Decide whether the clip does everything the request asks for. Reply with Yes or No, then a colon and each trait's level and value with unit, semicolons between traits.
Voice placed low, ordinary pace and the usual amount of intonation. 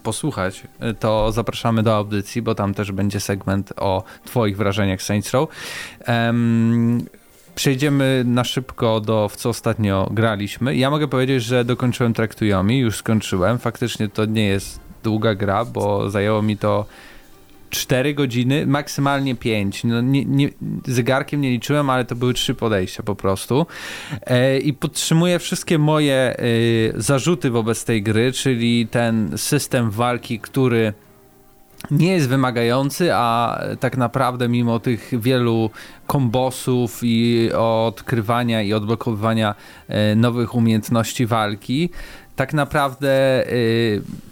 Yes: low, 120 Hz; average, 125 wpm; average, 3.1 semitones